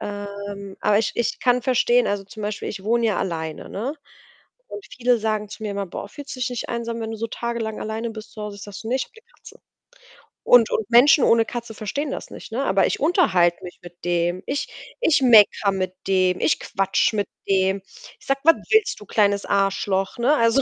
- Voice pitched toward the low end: No, high, 215 Hz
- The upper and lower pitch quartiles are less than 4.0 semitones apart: Yes, average, 3.4 semitones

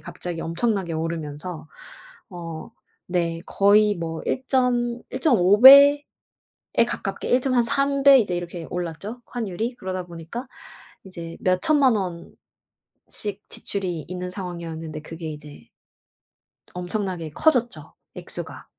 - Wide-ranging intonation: Yes, wide, 6.3 semitones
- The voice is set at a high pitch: No, medium, 180 Hz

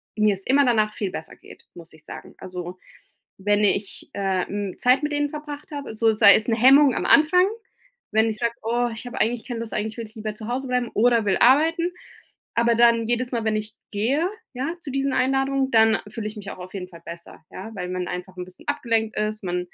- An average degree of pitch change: Yes, average, 4.0 semitones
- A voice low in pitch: No, high, 225 Hz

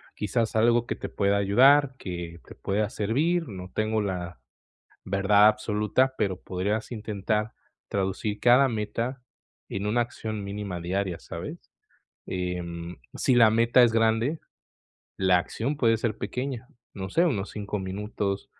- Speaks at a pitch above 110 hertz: No, low, 105 Hz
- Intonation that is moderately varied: Yes, average, 3.1 semitones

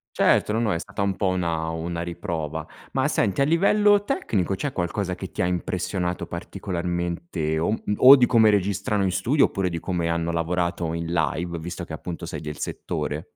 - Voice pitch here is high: No, very low, 90 Hz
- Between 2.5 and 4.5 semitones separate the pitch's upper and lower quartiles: Yes, average, 2.9 semitones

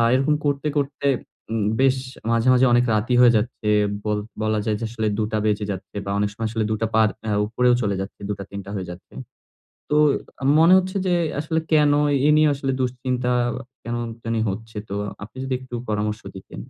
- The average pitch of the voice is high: No, low, 115 Hz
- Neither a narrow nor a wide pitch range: Yes, average, 3.8 semitones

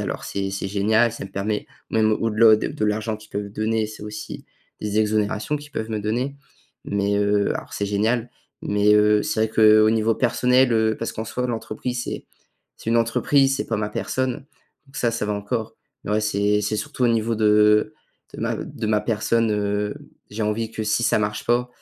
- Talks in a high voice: No, low, 110 Hz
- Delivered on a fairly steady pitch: Yes, narrow, 1.7 semitones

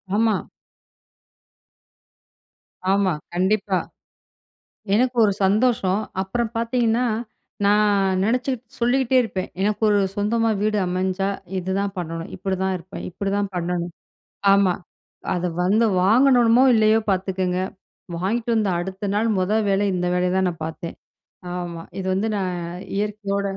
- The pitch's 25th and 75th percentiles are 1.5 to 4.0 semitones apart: Yes, average, 3.1 semitones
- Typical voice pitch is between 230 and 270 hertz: No, high, 200 Hz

